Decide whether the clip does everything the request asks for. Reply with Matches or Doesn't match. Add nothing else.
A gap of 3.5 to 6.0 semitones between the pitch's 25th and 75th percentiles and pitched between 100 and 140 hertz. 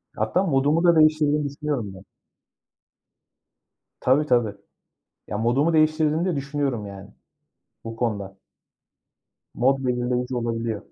Matches